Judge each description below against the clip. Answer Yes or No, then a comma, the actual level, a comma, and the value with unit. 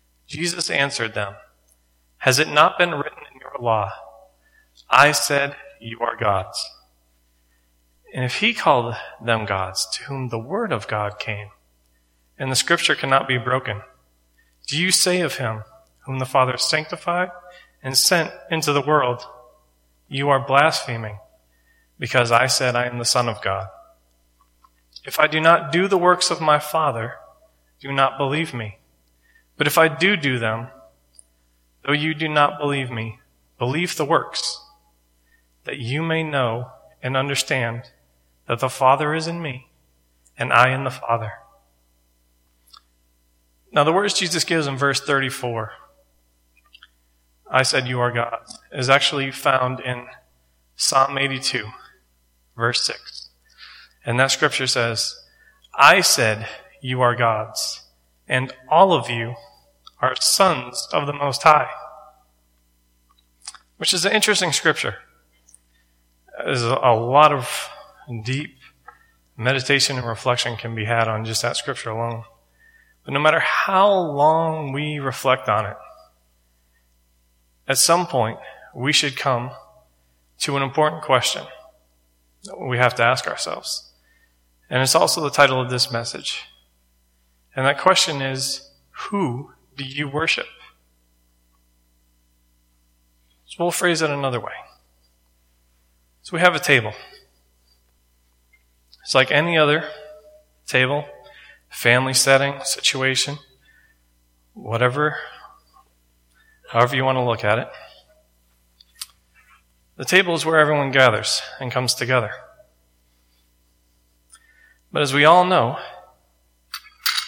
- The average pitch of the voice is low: Yes, low, 120 Hz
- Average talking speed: No, slow, 130 wpm